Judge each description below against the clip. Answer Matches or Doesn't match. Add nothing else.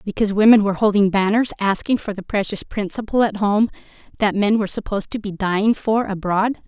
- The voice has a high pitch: Matches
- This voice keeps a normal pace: Matches